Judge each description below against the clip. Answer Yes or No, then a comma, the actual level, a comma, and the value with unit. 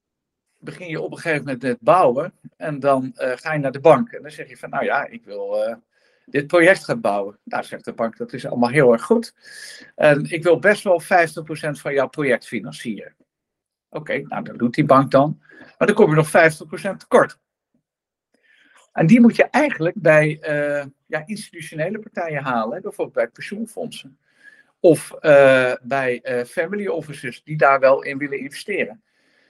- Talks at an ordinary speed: Yes, average, 190 wpm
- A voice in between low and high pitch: Yes, medium, 150 Hz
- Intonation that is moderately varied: Yes, average, 4.8 semitones